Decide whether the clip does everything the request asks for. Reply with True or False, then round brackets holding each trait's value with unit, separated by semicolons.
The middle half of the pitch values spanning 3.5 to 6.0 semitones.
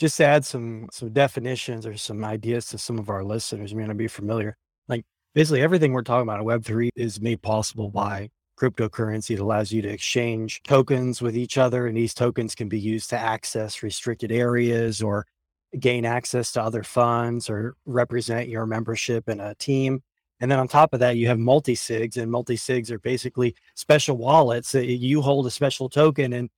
False (2.4 semitones)